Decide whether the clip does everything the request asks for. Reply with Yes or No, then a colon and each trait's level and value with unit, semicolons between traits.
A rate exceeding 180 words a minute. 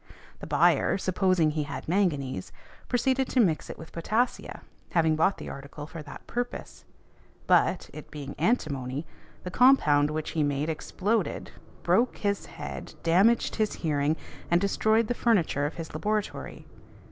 No: average, 145 wpm